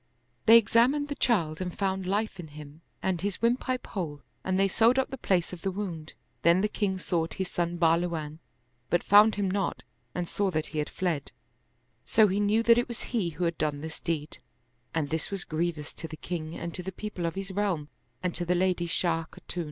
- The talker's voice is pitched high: No, medium, 180 Hz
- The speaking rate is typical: No, fast, 215 wpm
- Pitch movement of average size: Yes, average, 3.7 semitones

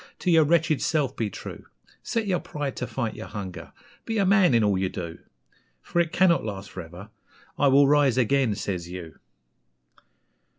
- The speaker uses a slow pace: No, average, 180 wpm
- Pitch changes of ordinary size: No, wide, 8.6 semitones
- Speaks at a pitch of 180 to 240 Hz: No, low, 130 Hz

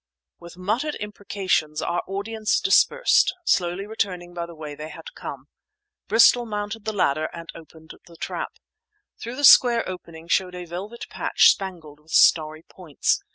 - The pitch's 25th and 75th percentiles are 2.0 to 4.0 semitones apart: No, average, 4.6 semitones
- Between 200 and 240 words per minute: No, average, 155 wpm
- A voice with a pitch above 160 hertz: Yes, medium, 185 Hz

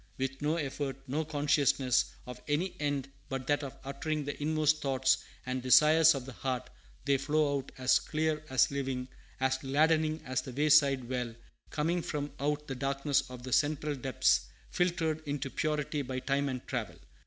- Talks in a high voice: No, medium, 140 Hz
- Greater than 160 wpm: Yes, average, 170 wpm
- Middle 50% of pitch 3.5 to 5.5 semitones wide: No, narrow, 2.5 semitones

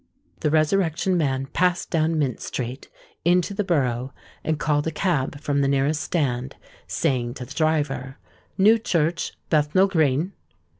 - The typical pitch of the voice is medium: Yes, medium, 150 Hz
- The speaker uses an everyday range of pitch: Yes, average, 4.0 semitones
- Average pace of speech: Yes, average, 145 wpm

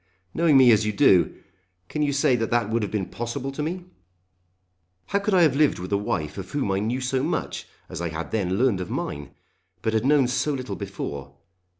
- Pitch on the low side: Yes, low, 120 Hz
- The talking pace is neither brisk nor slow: No, fast, 220 wpm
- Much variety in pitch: Yes, wide, 6.4 semitones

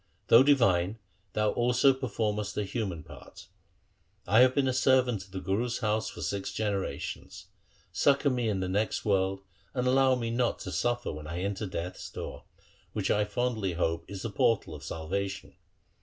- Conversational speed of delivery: Yes, average, 170 wpm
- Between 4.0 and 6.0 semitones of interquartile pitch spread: Yes, average, 4.5 semitones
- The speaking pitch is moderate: No, low, 105 Hz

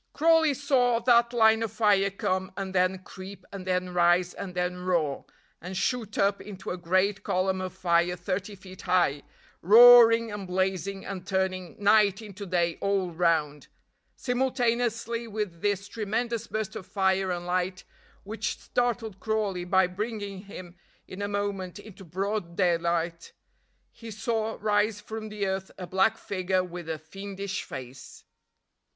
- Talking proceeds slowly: No, average, 150 wpm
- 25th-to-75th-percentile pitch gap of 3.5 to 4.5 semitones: No, average, 3.1 semitones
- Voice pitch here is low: No, high, 195 Hz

